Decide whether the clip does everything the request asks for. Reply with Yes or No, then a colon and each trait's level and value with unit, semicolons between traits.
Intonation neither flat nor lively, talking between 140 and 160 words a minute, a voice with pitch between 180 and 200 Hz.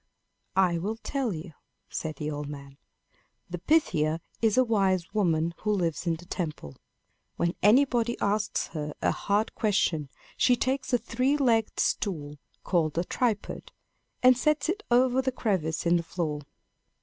No: wide, 6.9 semitones; average, 155 wpm; high, 190 Hz